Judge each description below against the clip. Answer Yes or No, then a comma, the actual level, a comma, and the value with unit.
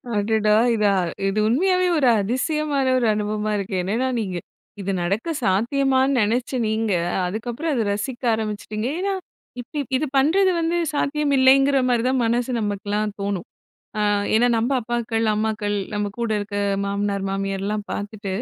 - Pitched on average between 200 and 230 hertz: Yes, high, 220 Hz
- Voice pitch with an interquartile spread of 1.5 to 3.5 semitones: No, average, 4.2 semitones